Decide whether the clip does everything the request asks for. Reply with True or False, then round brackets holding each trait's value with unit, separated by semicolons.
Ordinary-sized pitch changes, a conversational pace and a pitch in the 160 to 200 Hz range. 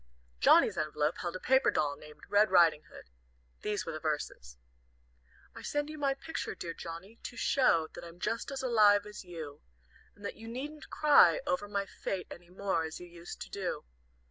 False (5.9 semitones; 190 wpm; 190 Hz)